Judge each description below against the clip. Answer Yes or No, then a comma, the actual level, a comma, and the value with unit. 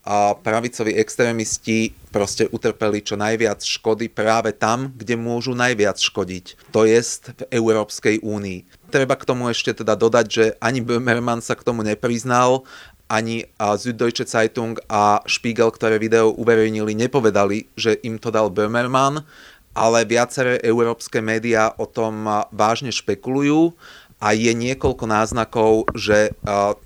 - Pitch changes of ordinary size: No, narrow, 1.9 semitones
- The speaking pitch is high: No, low, 110 Hz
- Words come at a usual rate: Yes, average, 135 wpm